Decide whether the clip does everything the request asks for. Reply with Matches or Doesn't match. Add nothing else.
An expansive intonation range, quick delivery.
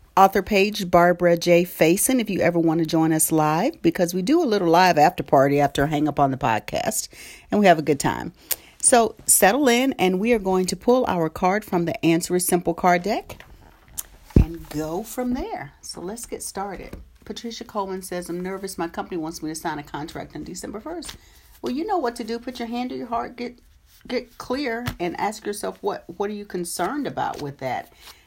Matches